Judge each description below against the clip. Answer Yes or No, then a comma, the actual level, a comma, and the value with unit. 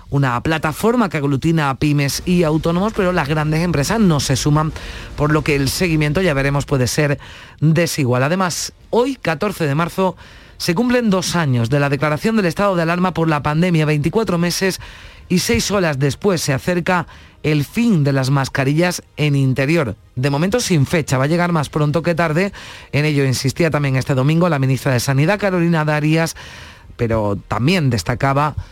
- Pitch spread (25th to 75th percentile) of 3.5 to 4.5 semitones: Yes, average, 4.2 semitones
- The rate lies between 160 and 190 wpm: Yes, average, 180 wpm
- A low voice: No, medium, 155 Hz